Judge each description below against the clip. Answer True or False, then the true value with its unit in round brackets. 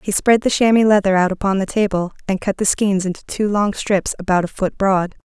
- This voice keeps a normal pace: False (240 wpm)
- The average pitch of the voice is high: True (195 Hz)